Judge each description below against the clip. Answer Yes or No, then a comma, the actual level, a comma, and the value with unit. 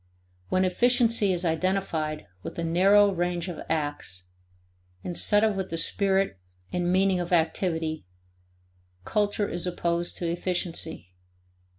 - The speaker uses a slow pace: Yes, slow, 120 wpm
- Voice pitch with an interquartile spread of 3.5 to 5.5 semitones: No, average, 2.9 semitones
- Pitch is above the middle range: No, medium, 175 Hz